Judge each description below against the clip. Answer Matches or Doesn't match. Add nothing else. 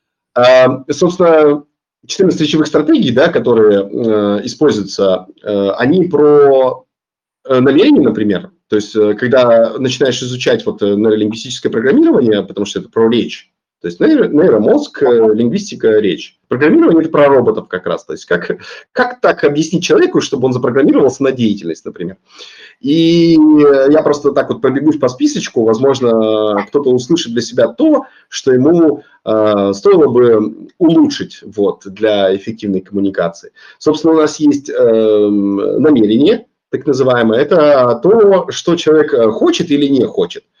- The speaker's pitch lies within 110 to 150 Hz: Matches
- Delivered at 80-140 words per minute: Matches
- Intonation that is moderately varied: Doesn't match